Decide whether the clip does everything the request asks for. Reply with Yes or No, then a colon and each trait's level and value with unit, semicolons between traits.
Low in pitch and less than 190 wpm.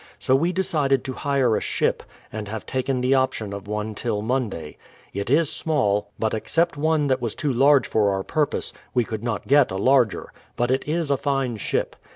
No: low, 130 Hz; fast, 205 wpm